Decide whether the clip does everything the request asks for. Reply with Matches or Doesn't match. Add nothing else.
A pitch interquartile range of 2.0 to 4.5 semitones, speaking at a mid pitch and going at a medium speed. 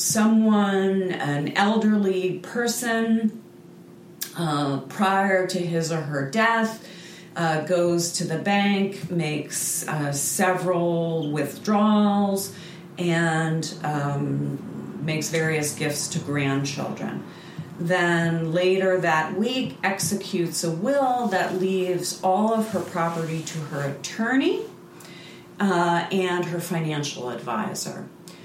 Doesn't match